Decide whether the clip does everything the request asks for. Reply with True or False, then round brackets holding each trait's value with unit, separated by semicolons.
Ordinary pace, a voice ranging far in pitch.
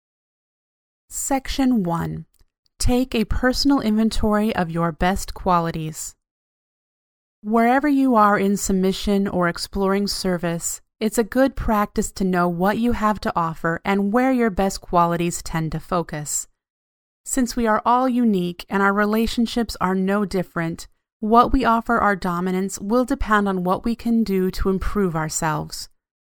False (145 wpm; 4.7 semitones)